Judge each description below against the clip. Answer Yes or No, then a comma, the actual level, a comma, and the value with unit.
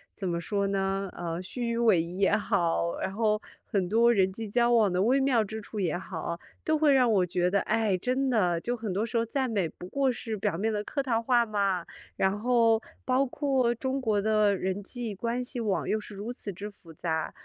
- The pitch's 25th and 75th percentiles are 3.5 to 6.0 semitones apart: Yes, average, 3.8 semitones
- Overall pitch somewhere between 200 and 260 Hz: Yes, high, 215 Hz